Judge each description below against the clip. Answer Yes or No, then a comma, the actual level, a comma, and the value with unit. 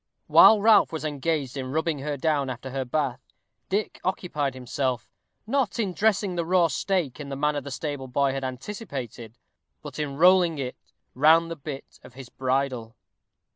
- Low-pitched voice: No, medium, 145 Hz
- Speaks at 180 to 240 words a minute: No, average, 170 wpm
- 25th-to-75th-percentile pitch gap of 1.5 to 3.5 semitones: No, average, 4.2 semitones